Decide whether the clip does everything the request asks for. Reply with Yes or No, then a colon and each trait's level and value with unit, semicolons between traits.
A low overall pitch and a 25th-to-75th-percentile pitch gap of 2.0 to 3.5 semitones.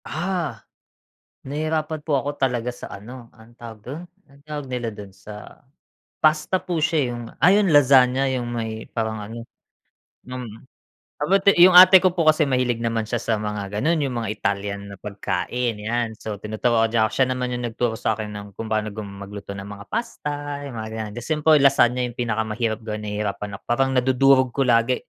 No: low, 120 Hz; average, 4.6 semitones